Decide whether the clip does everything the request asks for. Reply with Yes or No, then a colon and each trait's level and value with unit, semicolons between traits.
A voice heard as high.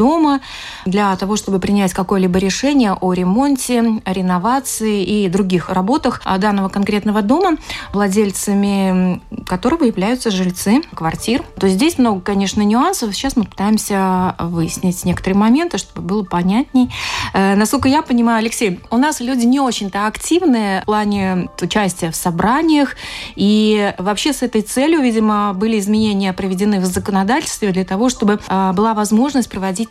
Yes: high, 210 Hz